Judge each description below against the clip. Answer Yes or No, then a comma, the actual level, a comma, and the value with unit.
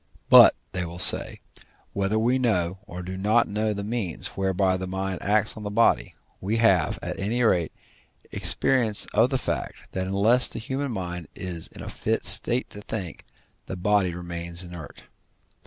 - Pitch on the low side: Yes, very low, 95 Hz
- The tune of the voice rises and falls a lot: No, average, 3.7 semitones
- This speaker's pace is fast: No, average, 170 wpm